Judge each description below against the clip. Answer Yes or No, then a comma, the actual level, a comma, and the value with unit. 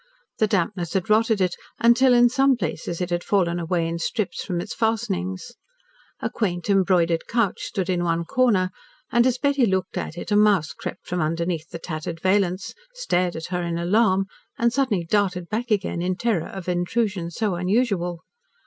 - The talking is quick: No, average, 180 wpm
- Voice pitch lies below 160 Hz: No, medium, 185 Hz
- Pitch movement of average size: Yes, average, 4.3 semitones